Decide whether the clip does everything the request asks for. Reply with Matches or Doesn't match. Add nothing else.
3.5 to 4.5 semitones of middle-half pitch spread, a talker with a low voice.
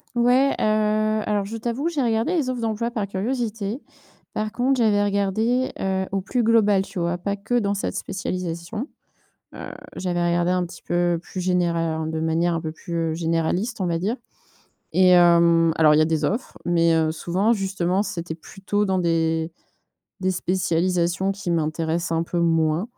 Doesn't match